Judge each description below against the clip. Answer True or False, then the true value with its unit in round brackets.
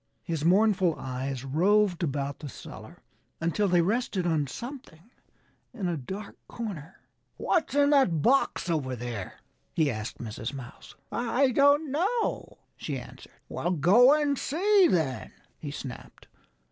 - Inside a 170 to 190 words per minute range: False (135 wpm)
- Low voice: False (175 Hz)